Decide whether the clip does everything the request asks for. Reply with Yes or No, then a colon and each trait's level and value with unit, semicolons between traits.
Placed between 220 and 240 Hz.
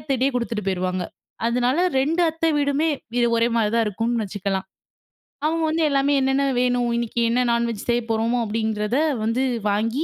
Yes: high, 235 Hz